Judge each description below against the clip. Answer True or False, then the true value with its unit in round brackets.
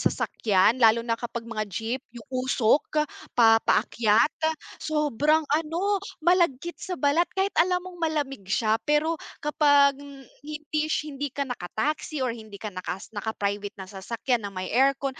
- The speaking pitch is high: True (265 Hz)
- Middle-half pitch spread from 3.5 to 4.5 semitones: False (5.5 semitones)